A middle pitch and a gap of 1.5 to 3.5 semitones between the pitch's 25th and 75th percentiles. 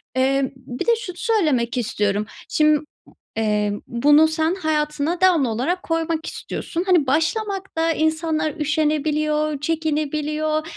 No: very high, 305 Hz; average, 2.9 semitones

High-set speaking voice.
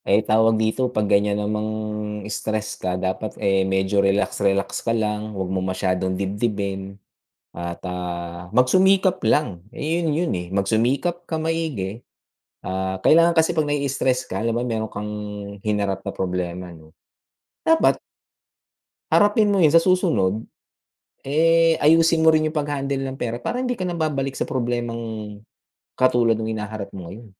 No: low, 110 Hz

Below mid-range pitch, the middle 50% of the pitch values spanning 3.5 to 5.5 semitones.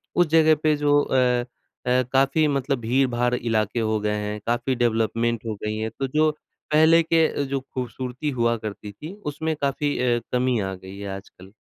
Yes: low, 125 Hz; average, 4.5 semitones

